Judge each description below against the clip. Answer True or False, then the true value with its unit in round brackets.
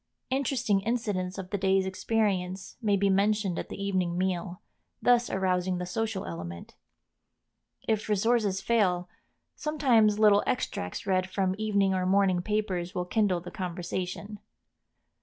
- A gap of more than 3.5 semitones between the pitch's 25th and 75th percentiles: False (2.8 semitones)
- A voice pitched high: True (195 Hz)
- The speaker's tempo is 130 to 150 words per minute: True (135 wpm)